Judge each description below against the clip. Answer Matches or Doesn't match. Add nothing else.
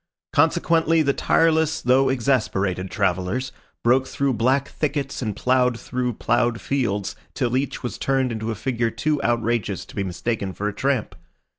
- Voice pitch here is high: Doesn't match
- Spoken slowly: Doesn't match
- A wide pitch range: Doesn't match